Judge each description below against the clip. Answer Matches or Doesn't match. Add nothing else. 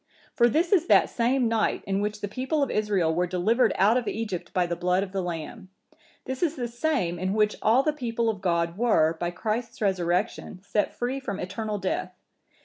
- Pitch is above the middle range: Matches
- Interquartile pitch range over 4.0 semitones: Matches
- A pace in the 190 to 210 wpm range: Matches